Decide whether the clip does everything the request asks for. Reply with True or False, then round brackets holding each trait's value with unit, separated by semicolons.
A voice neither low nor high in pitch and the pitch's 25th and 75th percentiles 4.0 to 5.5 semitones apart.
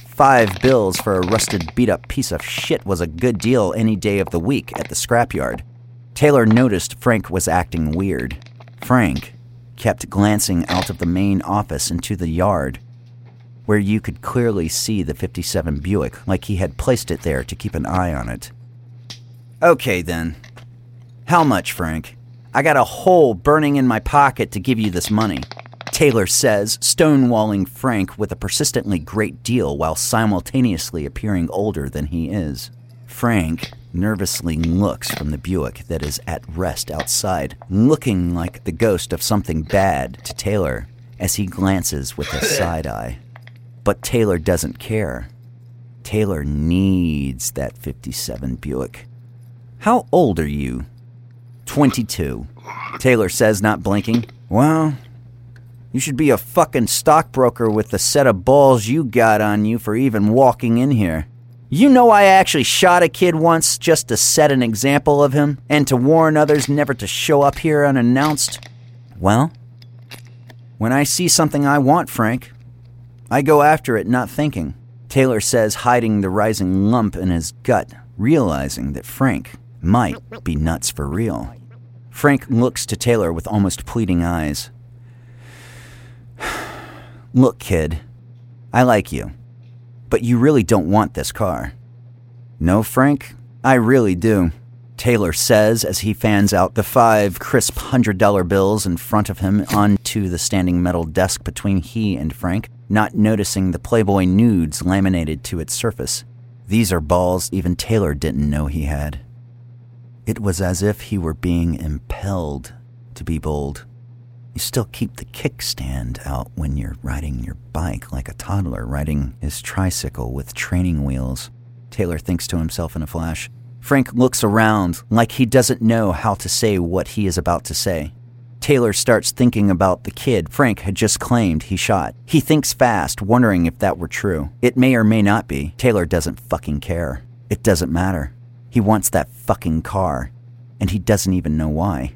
False (110 Hz; 4.8 semitones)